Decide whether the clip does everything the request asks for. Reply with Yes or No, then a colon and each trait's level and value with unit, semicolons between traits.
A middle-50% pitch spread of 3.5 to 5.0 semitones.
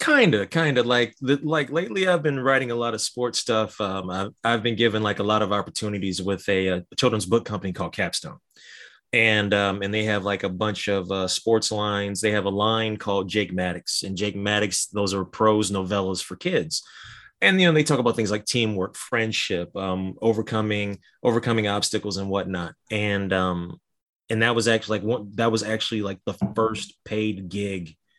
No: narrow, 2.6 semitones